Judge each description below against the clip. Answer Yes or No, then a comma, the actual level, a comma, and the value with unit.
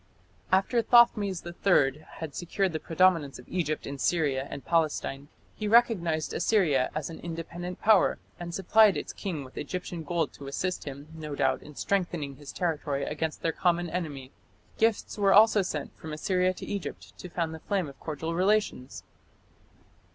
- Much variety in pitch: No, average, 4.0 semitones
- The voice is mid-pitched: Yes, medium, 170 Hz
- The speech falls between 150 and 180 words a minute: Yes, average, 165 wpm